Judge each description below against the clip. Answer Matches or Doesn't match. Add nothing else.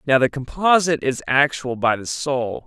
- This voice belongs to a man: Matches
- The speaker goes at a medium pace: Matches